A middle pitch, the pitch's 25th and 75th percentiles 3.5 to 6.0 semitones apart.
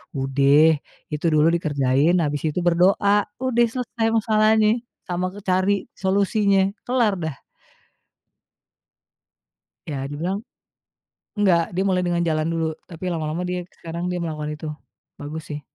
Yes: medium, 175 Hz; average, 4.4 semitones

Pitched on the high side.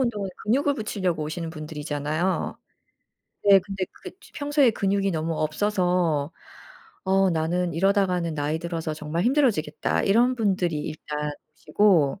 No: medium, 180 Hz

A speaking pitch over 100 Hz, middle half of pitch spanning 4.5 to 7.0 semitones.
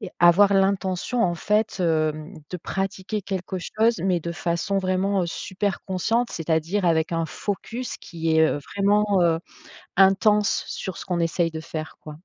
No: medium, 185 Hz; average, 3.3 semitones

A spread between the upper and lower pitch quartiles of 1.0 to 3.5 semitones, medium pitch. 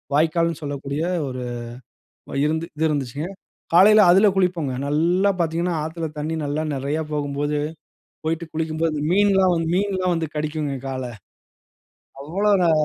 Yes: average, 3.1 semitones; medium, 160 Hz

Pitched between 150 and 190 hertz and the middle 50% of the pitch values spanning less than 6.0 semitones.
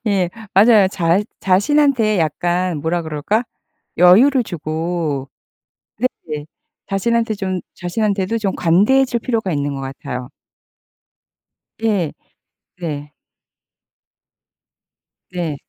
Yes: medium, 185 Hz; average, 5.3 semitones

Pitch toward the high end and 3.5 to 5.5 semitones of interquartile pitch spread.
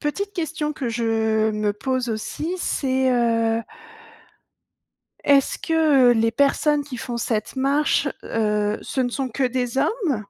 Yes: very high, 255 Hz; average, 4.2 semitones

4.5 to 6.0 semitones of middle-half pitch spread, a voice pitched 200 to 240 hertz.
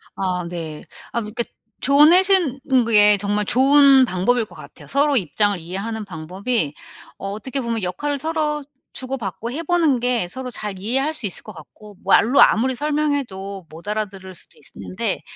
No: wide, 6.4 semitones; high, 220 Hz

